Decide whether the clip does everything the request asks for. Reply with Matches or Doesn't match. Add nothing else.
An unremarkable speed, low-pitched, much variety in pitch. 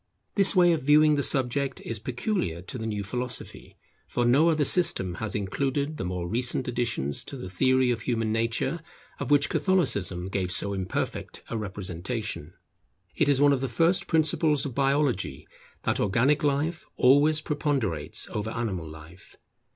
Matches